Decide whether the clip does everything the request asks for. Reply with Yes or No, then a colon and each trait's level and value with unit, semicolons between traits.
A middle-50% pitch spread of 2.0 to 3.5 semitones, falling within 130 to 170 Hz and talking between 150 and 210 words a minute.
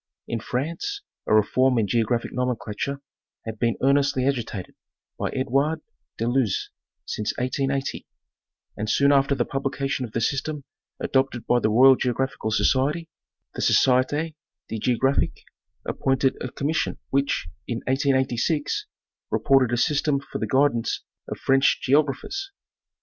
No: narrow, 2.5 semitones; low, 135 Hz; slow, 135 wpm